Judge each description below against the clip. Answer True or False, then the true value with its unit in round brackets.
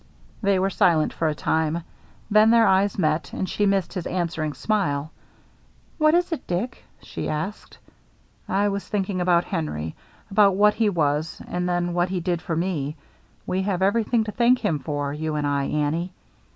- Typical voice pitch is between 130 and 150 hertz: False (180 Hz)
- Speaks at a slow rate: False (190 wpm)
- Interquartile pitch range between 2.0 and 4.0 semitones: False (4.4 semitones)